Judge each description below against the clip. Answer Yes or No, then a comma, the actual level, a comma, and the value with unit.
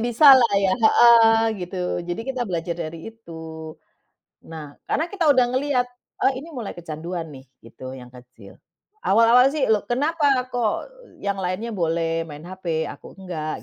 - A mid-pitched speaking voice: No, high, 195 Hz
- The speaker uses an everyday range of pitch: No, wide, 7.2 semitones